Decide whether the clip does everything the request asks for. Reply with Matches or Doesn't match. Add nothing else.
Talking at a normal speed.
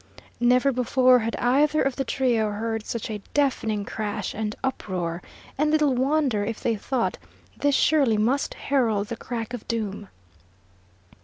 Matches